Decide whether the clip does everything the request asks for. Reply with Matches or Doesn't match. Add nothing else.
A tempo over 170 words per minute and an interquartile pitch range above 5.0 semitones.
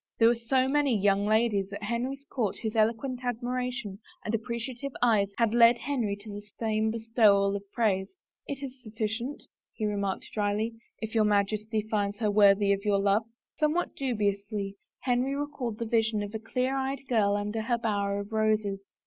Doesn't match